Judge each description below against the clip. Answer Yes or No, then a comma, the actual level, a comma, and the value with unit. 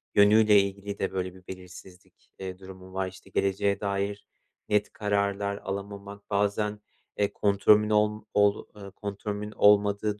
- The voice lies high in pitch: No, low, 100 Hz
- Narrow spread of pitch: Yes, narrow, 1.1 semitones